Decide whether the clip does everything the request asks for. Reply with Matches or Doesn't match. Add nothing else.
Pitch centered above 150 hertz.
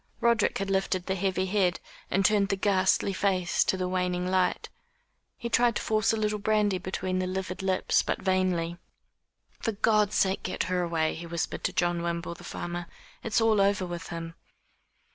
Matches